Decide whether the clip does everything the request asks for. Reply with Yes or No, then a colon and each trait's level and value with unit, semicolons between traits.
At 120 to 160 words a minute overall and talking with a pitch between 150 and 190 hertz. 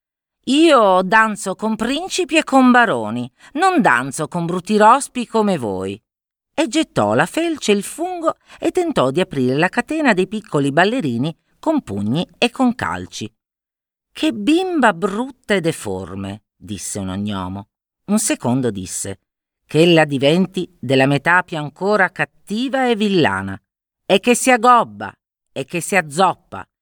Yes: average, 145 wpm; medium, 185 Hz